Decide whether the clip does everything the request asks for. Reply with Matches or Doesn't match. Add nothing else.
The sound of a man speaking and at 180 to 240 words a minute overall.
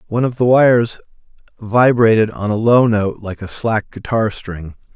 Doesn't match